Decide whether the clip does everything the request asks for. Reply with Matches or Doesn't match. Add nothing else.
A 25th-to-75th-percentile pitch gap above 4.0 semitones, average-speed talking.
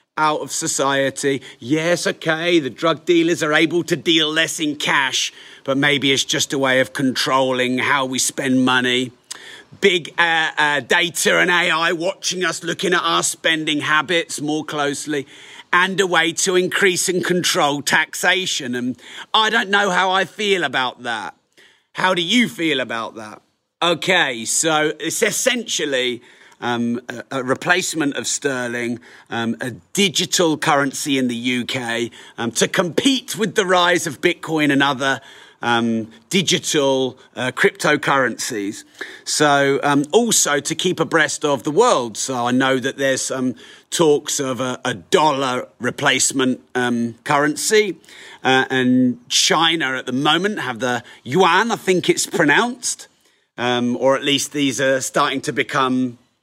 Matches